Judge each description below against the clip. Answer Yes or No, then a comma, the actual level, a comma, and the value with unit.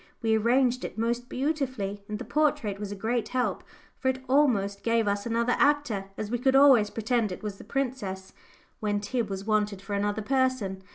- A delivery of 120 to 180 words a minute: No, average, 190 wpm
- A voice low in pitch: No, high, 225 Hz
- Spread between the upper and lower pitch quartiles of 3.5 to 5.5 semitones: Yes, average, 4.0 semitones